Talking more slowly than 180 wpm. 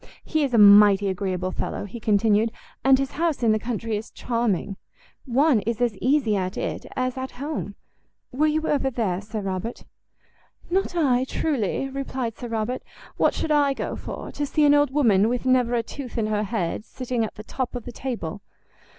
No: average, 195 wpm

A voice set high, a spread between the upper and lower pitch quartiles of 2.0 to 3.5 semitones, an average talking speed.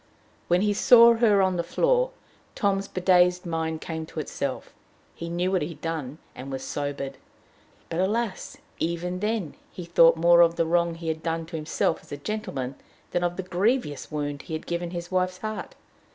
No: medium, 170 Hz; average, 2.8 semitones; average, 190 wpm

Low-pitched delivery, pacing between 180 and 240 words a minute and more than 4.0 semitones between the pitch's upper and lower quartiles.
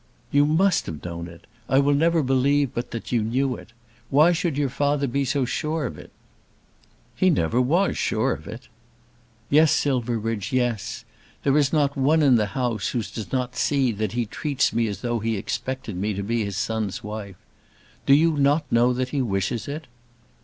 Yes: low, 125 Hz; average, 190 wpm; average, 4.4 semitones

